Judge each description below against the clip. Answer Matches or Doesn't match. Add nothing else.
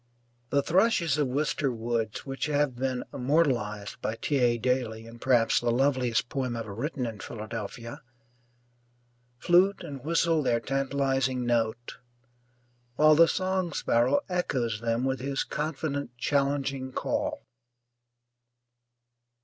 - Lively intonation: Doesn't match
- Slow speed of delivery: Matches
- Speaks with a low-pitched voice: Matches